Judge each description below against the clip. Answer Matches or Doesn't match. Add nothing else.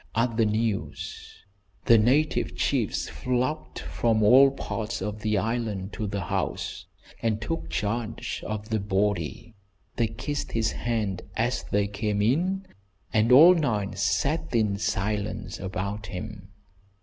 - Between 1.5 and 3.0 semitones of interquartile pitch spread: Matches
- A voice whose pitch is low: Matches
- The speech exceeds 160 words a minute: Doesn't match